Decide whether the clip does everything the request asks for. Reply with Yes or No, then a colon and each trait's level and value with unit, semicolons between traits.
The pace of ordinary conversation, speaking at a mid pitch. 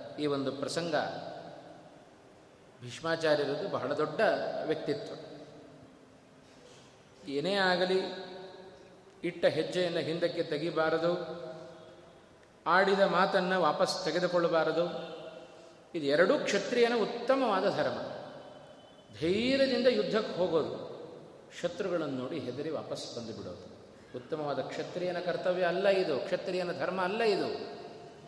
Yes: average, 85 wpm; medium, 170 Hz